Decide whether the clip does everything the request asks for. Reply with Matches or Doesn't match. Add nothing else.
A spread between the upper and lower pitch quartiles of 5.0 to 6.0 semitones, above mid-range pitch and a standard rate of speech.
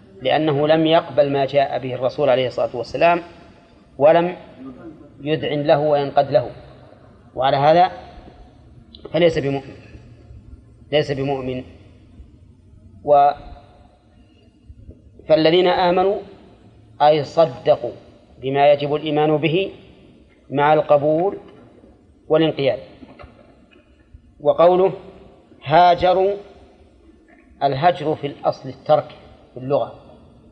Doesn't match